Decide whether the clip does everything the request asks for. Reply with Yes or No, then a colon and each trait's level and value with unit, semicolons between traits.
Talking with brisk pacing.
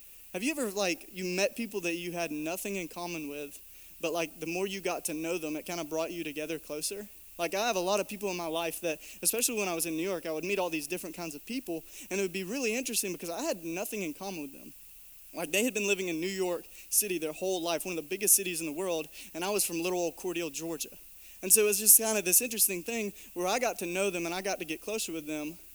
Yes: fast, 285 wpm